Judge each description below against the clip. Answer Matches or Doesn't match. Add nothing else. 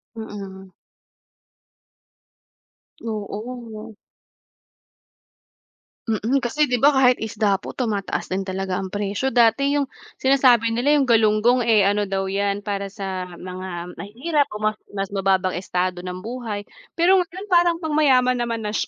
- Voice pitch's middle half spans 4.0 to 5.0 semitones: Matches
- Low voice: Doesn't match